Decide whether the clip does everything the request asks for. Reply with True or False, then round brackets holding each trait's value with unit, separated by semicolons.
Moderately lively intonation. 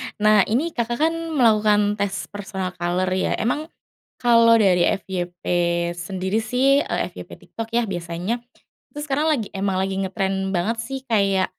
True (3.8 semitones)